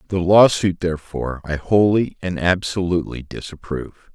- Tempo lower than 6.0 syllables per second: Yes, 5.3 syllables/s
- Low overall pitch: Yes, very low, 90 Hz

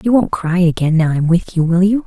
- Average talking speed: No, fast, 290 wpm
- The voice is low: No, medium, 180 Hz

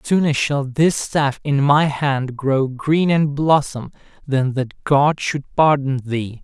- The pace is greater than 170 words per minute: No, average, 160 wpm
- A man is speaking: Yes, male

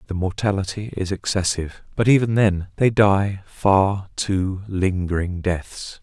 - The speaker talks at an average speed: No, slow, 130 wpm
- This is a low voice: Yes, very low, 95 Hz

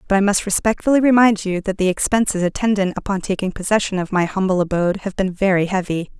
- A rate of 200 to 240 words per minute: Yes, fast, 205 wpm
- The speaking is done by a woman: Yes, female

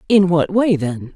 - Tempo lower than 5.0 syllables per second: Yes, 4.1 syllables/s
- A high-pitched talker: No, medium, 175 Hz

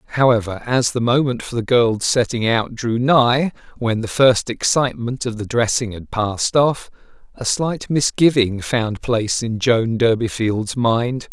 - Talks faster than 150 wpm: Yes, average, 160 wpm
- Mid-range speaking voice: No, low, 120 Hz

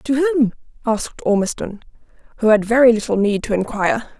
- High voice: Yes, high, 230 Hz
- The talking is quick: No, average, 155 wpm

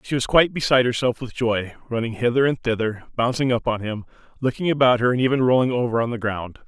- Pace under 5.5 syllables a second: No, 6.4 syllables/s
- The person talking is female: No, male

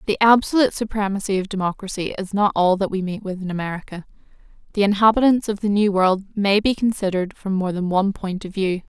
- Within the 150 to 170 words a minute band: No, average, 200 wpm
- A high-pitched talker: Yes, high, 200 Hz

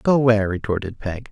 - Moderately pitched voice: No, low, 110 Hz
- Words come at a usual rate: Yes, average, 180 wpm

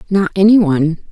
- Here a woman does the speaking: Yes, female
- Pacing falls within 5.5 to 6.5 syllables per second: Yes, 5.9 syllables/s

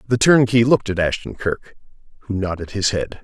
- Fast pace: No, average, 185 wpm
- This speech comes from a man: Yes, male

